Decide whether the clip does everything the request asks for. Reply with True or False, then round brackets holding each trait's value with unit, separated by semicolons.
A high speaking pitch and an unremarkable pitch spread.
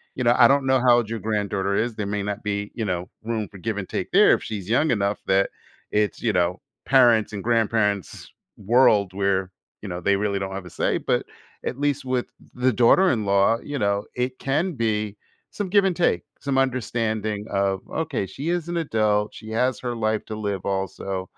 False (110 Hz; 4.0 semitones)